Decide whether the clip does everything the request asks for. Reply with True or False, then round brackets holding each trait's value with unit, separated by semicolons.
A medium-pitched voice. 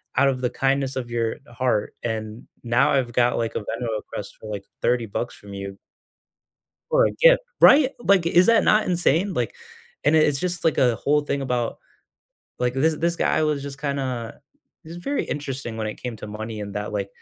False (130 Hz)